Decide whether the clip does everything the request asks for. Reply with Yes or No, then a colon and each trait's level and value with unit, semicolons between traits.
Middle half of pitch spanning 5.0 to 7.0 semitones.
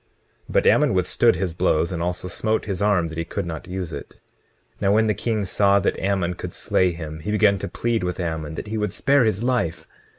No: average, 3.7 semitones